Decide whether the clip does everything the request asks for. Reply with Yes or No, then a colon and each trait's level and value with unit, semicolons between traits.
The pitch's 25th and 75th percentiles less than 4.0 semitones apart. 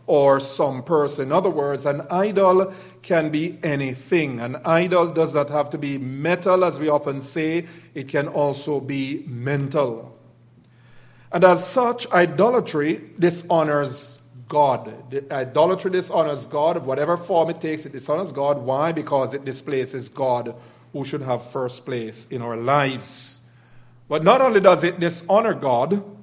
No: average, 4.3 semitones